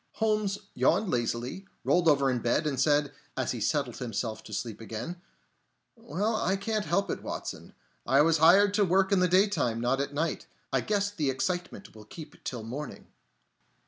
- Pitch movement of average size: No, wide, 7.6 semitones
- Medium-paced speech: Yes, average, 175 wpm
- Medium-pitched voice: Yes, medium, 155 Hz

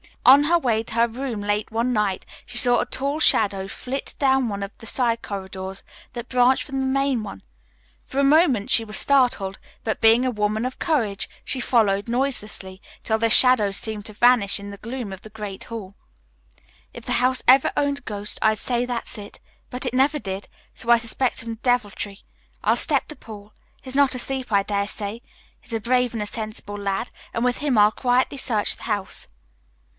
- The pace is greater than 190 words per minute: Yes, average, 200 wpm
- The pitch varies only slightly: No, average, 3.7 semitones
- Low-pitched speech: No, high, 230 Hz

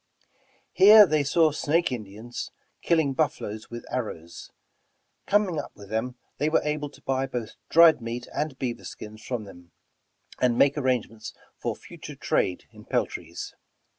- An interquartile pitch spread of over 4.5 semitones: Yes, wide, 5.4 semitones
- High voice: No, low, 130 Hz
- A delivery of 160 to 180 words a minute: No, average, 145 wpm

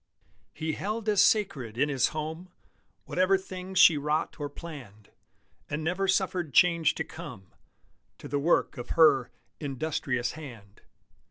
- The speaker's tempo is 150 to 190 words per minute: No, average, 140 wpm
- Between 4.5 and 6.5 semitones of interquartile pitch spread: Yes, average, 5.0 semitones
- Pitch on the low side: No, medium, 155 Hz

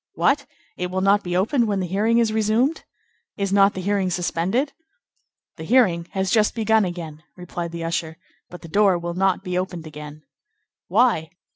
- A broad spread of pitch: No, average, 3.9 semitones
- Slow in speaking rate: No, average, 180 wpm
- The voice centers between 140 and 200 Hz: Yes, high, 190 Hz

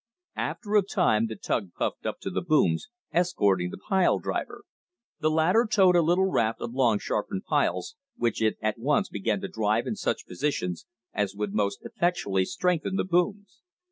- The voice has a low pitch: No, medium, 145 Hz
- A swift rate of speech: No, average, 175 wpm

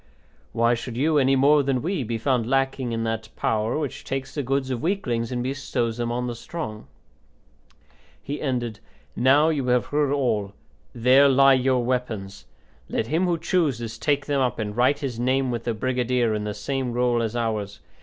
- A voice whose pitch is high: No, low, 125 Hz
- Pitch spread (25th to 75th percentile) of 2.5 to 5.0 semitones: Yes, average, 2.9 semitones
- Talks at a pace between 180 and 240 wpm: Yes, average, 185 wpm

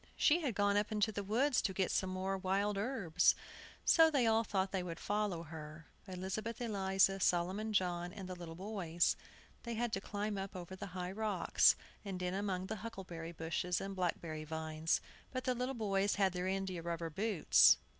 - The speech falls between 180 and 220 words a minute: Yes, average, 185 wpm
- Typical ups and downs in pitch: Yes, average, 3.1 semitones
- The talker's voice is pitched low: No, high, 190 Hz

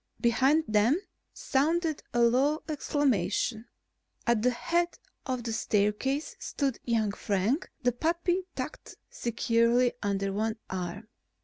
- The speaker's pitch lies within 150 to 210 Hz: No, high, 240 Hz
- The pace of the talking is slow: Yes, slow, 115 wpm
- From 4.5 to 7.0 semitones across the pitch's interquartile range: Yes, average, 5.1 semitones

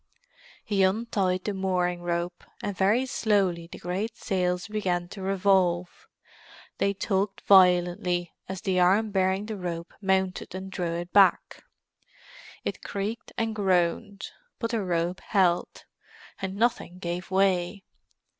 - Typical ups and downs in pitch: No, narrow, 2.1 semitones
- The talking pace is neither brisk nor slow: No, slow, 130 wpm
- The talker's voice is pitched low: No, high, 190 Hz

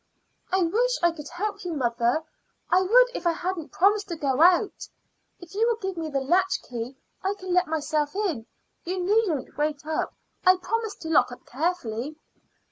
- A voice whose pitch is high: Yes, very high, 350 Hz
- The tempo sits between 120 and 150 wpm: No, average, 180 wpm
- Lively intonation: No, average, 4.5 semitones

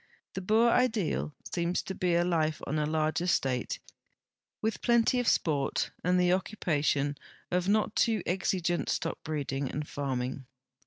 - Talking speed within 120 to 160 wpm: Yes, average, 140 wpm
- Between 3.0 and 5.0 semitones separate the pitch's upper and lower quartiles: Yes, average, 4.6 semitones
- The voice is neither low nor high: Yes, medium, 170 Hz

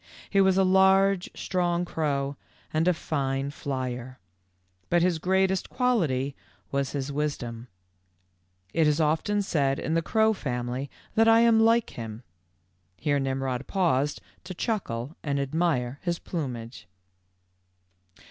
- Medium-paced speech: No, slow, 130 wpm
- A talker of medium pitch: Yes, medium, 155 Hz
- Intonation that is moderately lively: No, wide, 5.8 semitones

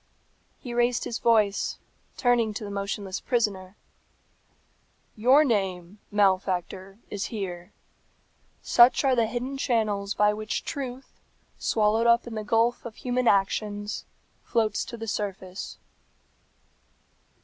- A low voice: No, high, 215 Hz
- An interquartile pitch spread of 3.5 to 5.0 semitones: No, average, 3.1 semitones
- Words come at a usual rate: No, slow, 115 wpm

